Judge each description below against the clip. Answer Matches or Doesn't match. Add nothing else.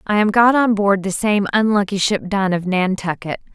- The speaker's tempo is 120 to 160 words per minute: Doesn't match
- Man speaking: Doesn't match